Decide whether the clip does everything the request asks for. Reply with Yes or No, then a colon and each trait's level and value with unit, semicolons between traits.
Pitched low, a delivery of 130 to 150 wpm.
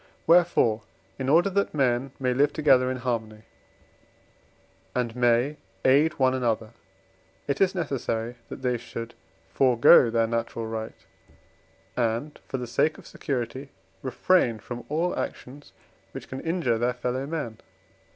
Yes: low, 125 Hz; slow, 135 wpm